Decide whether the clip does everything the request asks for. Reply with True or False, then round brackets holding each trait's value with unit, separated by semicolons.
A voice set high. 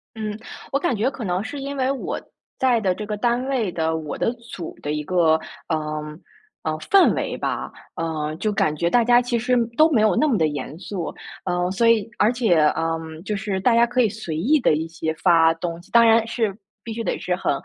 True (210 Hz)